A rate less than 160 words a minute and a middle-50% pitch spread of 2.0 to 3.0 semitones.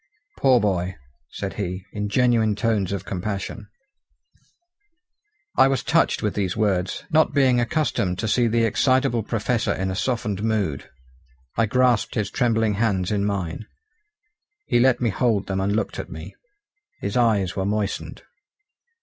No: average, 150 wpm; average, 3.5 semitones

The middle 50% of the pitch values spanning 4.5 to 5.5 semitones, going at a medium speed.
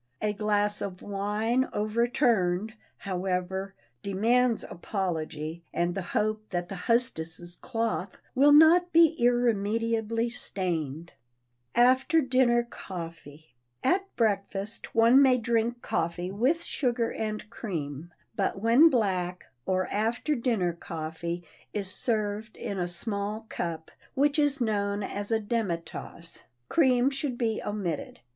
No: average, 4.8 semitones; slow, 125 wpm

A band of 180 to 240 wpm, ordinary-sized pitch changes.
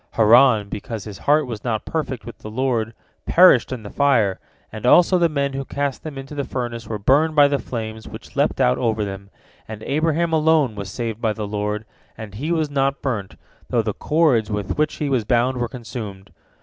Yes: fast, 205 wpm; average, 4.8 semitones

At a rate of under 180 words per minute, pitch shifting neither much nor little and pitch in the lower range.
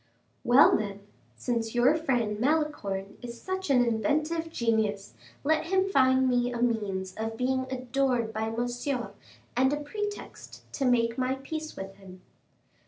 No: average, 145 wpm; average, 4.2 semitones; high, 245 Hz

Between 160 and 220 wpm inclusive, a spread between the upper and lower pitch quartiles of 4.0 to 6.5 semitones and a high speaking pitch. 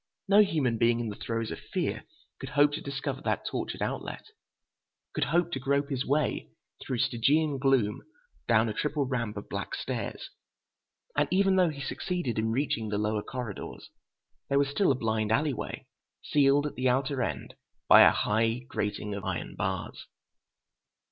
No: average, 170 wpm; average, 4.5 semitones; low, 130 Hz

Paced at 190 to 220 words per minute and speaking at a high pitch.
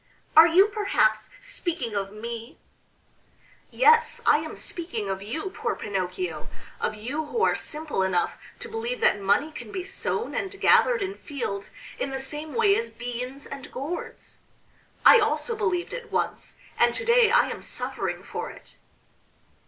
No: average, 160 wpm; very high, 300 Hz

